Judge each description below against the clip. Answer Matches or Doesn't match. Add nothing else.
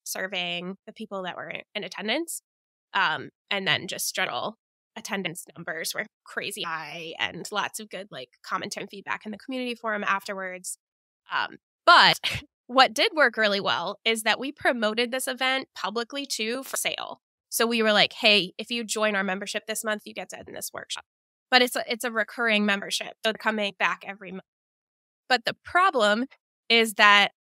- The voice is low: Doesn't match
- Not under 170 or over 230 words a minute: Matches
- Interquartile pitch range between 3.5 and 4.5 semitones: Matches